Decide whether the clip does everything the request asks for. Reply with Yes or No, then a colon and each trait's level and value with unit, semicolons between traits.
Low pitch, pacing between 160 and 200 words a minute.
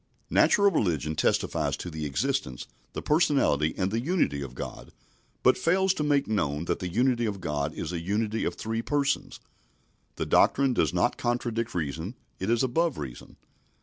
Yes: low, 110 Hz; average, 170 wpm